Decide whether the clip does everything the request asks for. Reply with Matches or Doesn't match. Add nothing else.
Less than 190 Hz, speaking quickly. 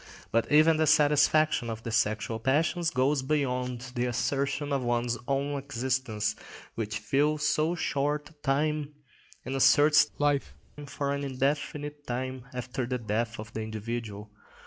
Doesn't match